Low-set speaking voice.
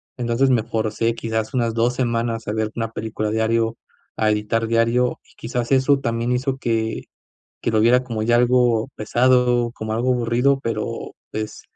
Yes: low, 115 Hz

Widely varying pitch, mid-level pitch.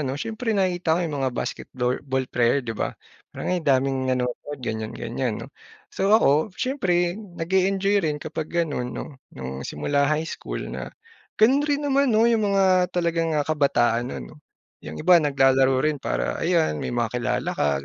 Yes: wide, 6.3 semitones; medium, 150 Hz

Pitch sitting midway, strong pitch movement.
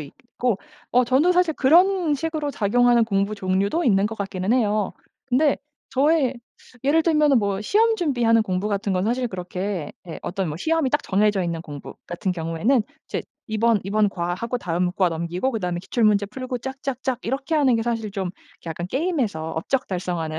No: high, 220 Hz; wide, 6.2 semitones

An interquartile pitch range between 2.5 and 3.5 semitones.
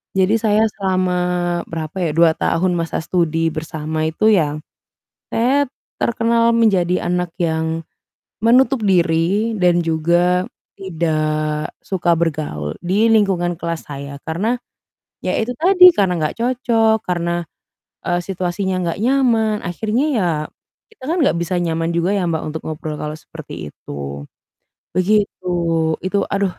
No: average, 4.7 semitones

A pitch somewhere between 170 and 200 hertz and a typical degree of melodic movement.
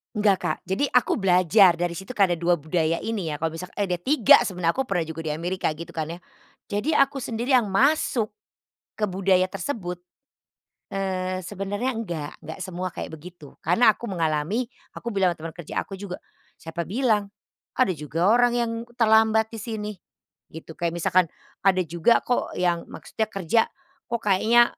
Yes: high, 190 Hz; average, 4.4 semitones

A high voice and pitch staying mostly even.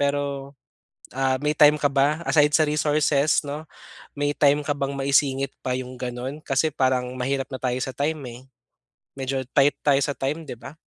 No: medium, 140 Hz; narrow, 1.9 semitones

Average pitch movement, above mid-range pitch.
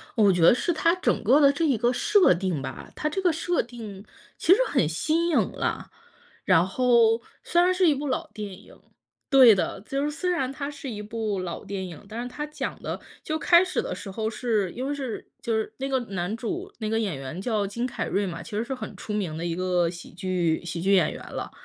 No: wide, 7.1 semitones; high, 225 Hz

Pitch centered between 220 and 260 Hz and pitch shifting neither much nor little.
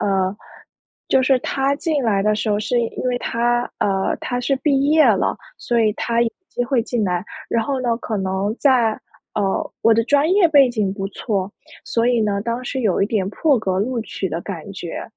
Yes: high, 230 Hz; average, 4.3 semitones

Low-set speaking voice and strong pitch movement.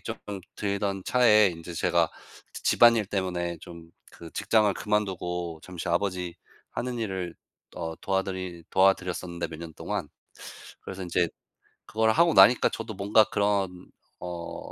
No: very low, 95 Hz; average, 2.9 semitones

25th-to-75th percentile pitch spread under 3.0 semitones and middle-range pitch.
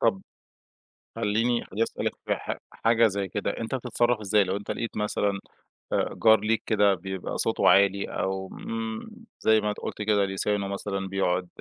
No: narrow, 2.4 semitones; low, 105 Hz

